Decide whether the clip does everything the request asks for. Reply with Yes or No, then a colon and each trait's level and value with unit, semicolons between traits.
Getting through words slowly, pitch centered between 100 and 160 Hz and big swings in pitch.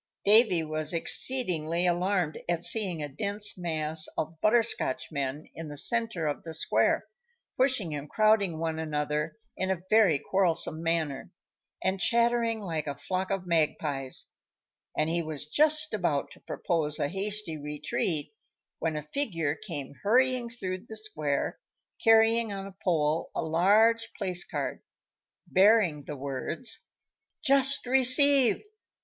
No: slow, 130 wpm; medium, 175 Hz; wide, 6.0 semitones